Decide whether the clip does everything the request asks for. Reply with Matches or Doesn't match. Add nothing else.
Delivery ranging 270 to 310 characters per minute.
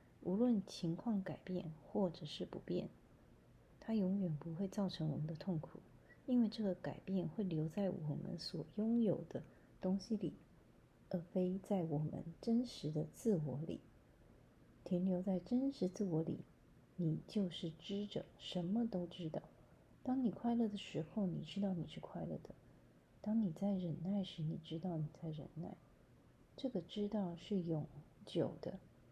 Doesn't match